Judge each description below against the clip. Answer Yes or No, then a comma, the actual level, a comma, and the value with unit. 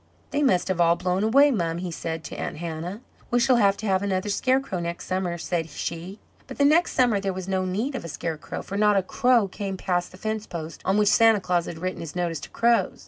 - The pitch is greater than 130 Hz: Yes, high, 190 Hz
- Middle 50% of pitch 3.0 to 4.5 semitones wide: Yes, average, 4.2 semitones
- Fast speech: Yes, fast, 245 wpm